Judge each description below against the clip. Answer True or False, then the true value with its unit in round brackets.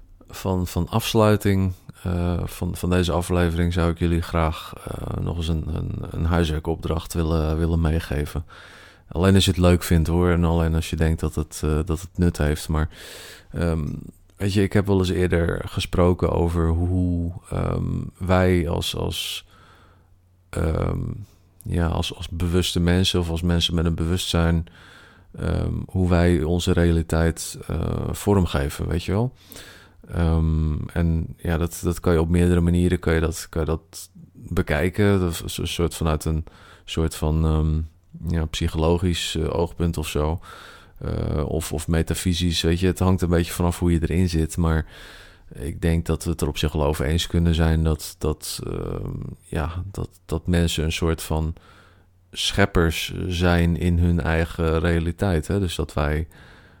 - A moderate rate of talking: True (170 wpm)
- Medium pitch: False (85 Hz)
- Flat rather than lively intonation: True (1.9 semitones)